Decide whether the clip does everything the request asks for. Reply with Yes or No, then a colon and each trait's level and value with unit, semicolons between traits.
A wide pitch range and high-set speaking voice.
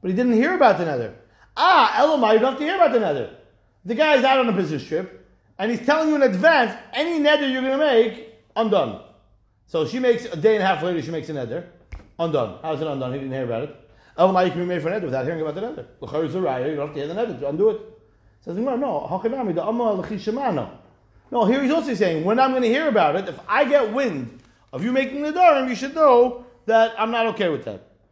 Yes: wide, 8.3 semitones; high, 225 Hz